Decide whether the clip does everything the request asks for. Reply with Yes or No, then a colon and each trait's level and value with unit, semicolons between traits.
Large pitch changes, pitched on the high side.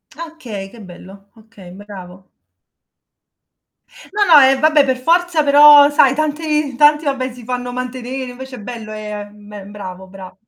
Yes: wide, 6.0 semitones; very high, 250 Hz